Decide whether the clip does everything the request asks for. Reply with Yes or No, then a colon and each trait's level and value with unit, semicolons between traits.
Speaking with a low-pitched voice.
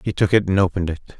Yes: very low, 95 Hz